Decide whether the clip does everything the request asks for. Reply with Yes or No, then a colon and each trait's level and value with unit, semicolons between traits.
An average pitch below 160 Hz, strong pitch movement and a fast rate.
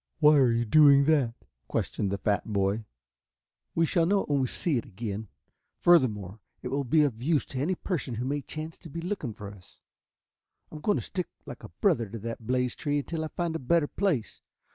Yes: medium, 140 Hz; wide, 5.9 semitones; fast, 215 wpm